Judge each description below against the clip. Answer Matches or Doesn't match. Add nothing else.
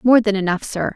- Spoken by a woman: Matches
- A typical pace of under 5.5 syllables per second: Doesn't match